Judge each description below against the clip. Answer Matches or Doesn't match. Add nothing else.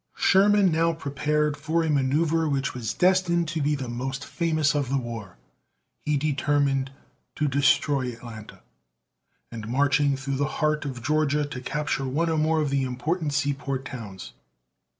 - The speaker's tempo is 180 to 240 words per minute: Doesn't match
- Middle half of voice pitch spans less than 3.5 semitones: Matches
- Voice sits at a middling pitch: Matches